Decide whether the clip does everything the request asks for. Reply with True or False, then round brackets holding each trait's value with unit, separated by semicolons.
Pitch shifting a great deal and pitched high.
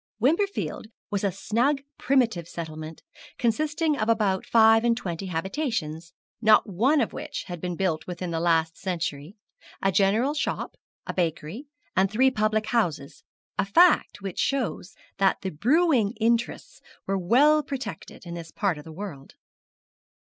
True (6.0 semitones; 200 Hz)